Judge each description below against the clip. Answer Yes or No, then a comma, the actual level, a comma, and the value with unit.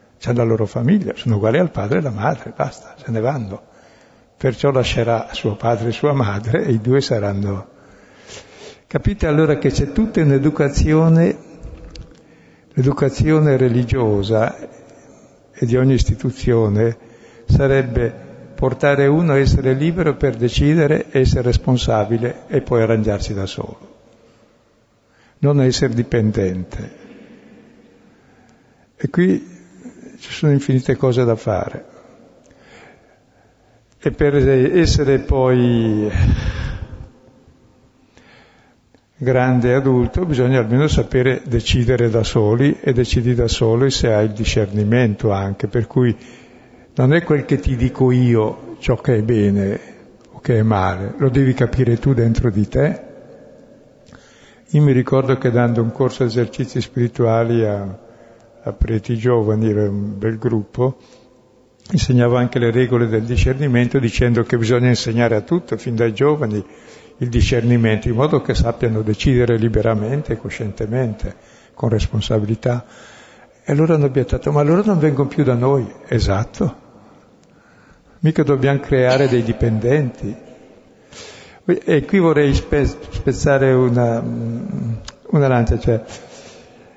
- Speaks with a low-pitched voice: Yes, low, 120 Hz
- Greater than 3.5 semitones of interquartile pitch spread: No, average, 3.2 semitones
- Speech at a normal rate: Yes, average, 125 wpm